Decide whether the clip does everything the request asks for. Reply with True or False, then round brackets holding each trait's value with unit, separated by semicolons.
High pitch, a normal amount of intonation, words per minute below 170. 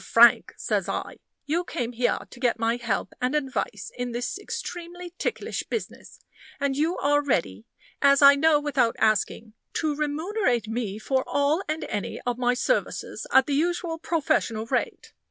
True (275 Hz; 4.8 semitones; 160 wpm)